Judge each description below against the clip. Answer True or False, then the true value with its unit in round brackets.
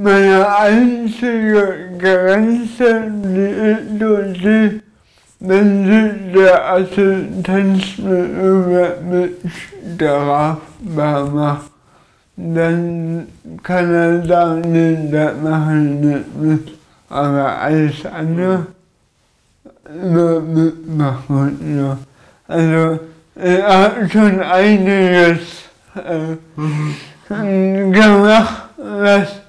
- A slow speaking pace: True (85 wpm)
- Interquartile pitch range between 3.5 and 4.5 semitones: True (3.8 semitones)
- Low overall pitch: False (180 Hz)